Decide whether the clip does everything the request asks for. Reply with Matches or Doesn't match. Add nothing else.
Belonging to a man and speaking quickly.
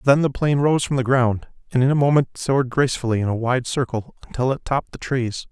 Matches